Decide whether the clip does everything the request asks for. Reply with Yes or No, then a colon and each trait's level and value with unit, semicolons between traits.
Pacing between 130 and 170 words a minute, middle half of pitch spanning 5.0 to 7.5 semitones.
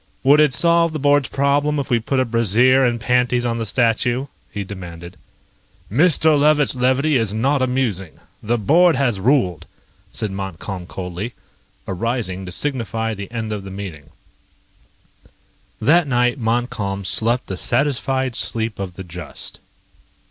Yes: average, 145 wpm; average, 5.3 semitones